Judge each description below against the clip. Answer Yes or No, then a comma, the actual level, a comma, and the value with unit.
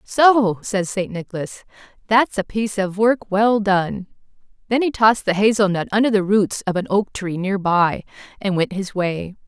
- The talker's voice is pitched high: Yes, high, 200 Hz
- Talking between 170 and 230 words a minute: Yes, average, 190 wpm